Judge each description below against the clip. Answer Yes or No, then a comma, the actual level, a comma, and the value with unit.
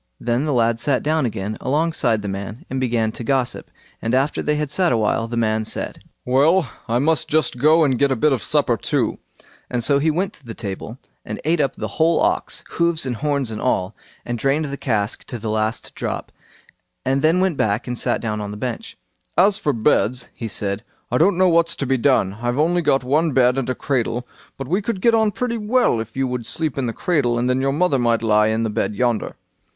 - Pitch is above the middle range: No, low, 130 Hz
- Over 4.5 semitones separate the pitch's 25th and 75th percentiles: Yes, average, 5.2 semitones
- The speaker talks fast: Yes, fast, 225 wpm